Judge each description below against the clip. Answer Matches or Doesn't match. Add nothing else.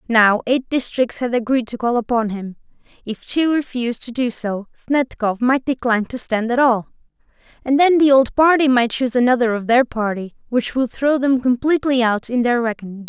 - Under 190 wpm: Doesn't match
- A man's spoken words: Doesn't match